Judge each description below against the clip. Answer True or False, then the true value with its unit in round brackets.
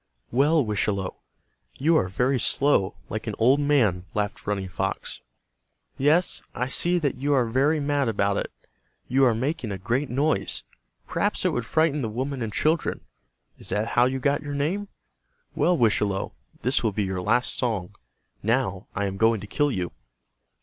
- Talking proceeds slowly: False (170 wpm)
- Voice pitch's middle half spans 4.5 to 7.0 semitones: True (5.6 semitones)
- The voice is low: True (125 Hz)